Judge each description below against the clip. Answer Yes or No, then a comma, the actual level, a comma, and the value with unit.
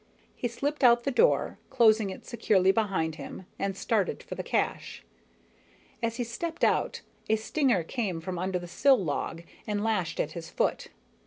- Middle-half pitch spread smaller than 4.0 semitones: No, average, 4.6 semitones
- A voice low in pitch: No, high, 215 Hz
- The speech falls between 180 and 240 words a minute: No, average, 170 wpm